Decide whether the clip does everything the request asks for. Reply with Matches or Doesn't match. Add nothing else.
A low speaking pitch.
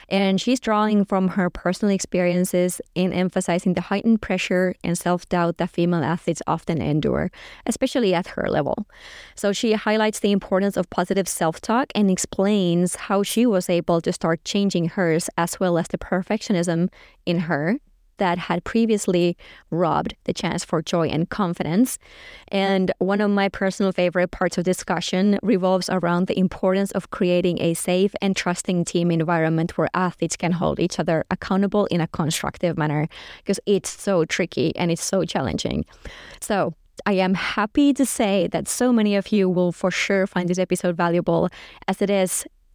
Doesn't match